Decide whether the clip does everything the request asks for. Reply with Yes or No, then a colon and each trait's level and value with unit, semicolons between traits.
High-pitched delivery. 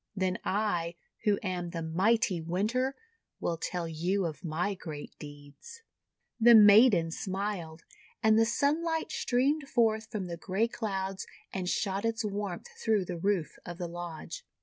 Yes: high, 195 Hz